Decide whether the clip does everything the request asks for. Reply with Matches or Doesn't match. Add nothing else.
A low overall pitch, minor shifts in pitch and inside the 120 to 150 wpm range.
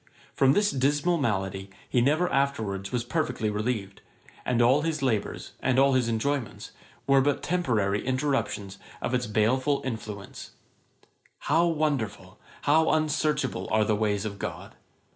Doesn't match